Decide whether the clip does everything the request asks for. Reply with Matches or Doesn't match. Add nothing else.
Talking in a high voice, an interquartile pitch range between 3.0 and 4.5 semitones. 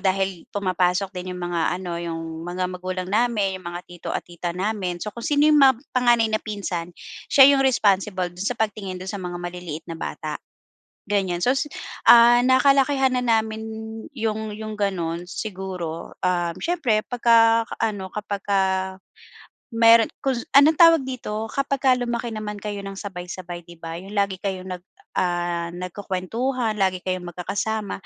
Matches